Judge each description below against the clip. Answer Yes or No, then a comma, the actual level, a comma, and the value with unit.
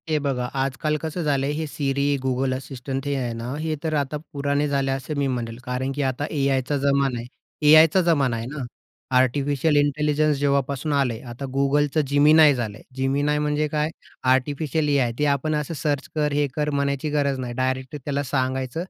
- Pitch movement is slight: Yes, narrow, 2.1 semitones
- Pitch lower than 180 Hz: Yes, medium, 140 Hz